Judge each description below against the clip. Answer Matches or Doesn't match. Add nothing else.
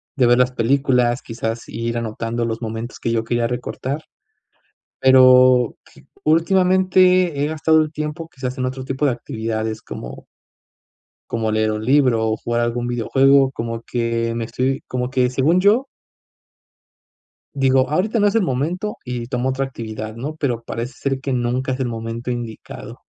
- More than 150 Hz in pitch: Doesn't match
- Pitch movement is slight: Doesn't match